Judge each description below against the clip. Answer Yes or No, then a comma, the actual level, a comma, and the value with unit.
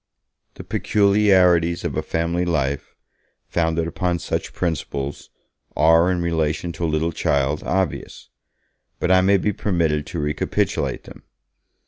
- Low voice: Yes, very low, 85 Hz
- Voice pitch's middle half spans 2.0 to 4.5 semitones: Yes, narrow, 2.6 semitones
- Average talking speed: No, slow, 130 wpm